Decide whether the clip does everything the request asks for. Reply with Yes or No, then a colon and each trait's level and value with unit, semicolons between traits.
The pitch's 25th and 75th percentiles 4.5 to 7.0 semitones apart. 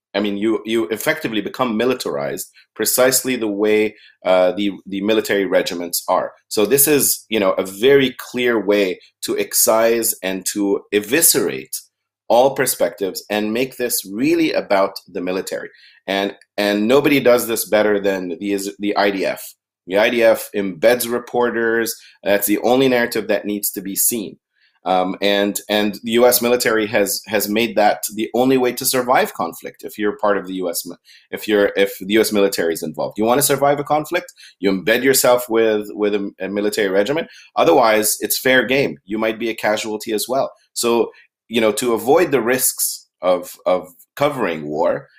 No: average, 3.2 semitones